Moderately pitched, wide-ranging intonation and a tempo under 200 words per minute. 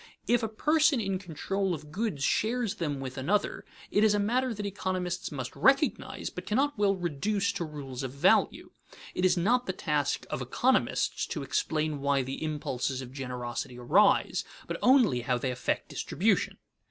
Yes: medium, 175 Hz; wide, 7.4 semitones; average, 170 wpm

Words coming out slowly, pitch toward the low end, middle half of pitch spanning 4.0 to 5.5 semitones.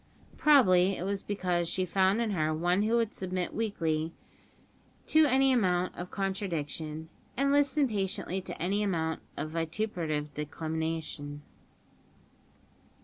No: slow, 125 wpm; medium, 185 Hz; average, 4.4 semitones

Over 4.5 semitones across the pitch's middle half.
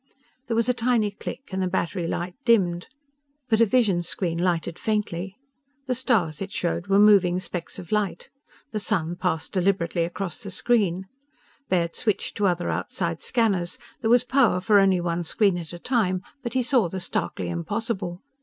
No: average, 4.0 semitones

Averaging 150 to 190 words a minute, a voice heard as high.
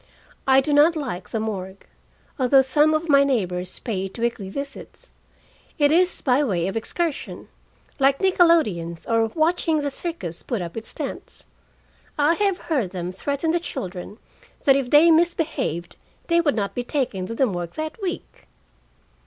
Yes: average, 160 wpm; very high, 270 Hz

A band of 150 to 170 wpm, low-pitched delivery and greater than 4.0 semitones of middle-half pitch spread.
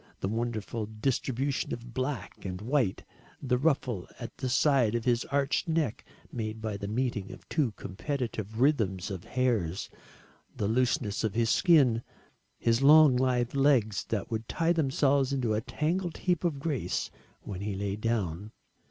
Yes: average, 155 wpm; low, 120 Hz; average, 4.4 semitones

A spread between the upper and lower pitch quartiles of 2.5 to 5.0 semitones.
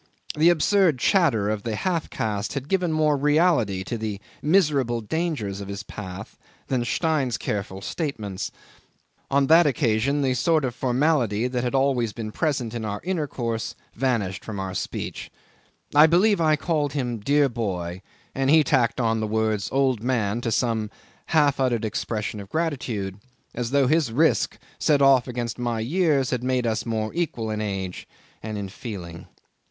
No: wide, 5.4 semitones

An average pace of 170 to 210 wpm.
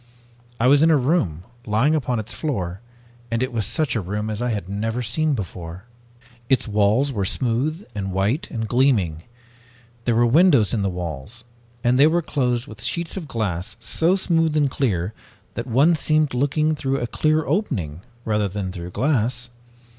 Yes: average, 175 wpm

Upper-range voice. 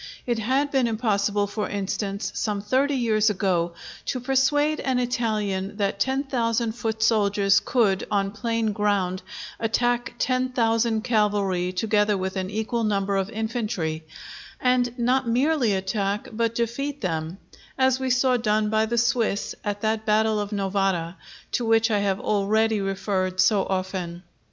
Yes: high, 215 Hz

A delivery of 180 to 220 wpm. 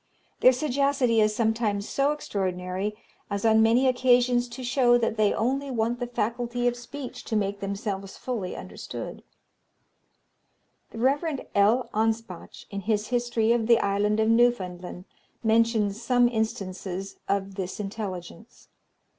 No: slow, 135 wpm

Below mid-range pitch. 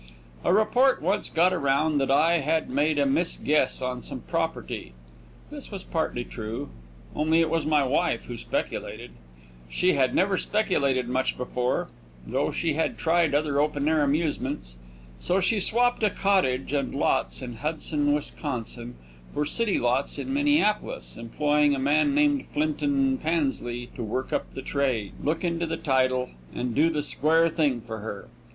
No: medium, 150 Hz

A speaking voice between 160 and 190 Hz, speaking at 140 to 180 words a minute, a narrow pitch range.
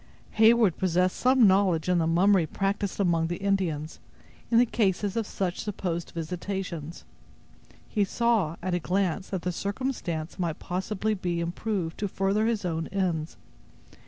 No: medium, 185 Hz; average, 150 wpm; average, 3.1 semitones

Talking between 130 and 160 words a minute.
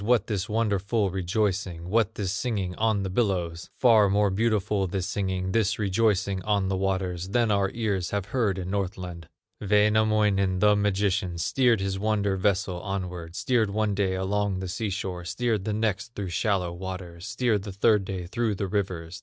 No: average, 170 wpm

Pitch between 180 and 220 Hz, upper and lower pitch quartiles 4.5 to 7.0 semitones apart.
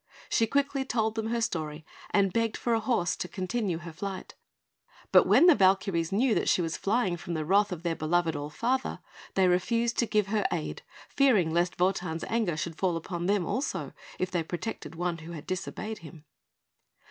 Yes: medium, 185 Hz; average, 4.8 semitones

